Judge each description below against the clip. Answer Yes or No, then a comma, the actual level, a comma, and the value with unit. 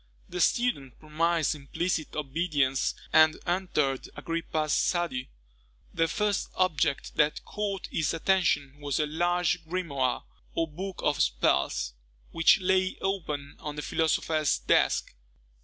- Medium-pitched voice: Yes, medium, 160 Hz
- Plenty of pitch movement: No, average, 3.6 semitones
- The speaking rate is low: Yes, slow, 120 wpm